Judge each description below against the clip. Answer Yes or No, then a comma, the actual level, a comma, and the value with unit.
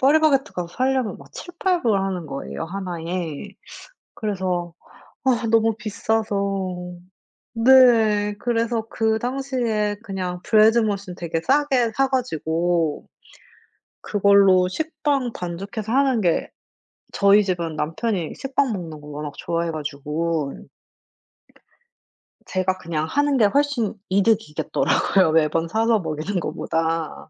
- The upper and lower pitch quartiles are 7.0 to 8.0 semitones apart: No, wide, 5.6 semitones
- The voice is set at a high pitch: Yes, high, 200 Hz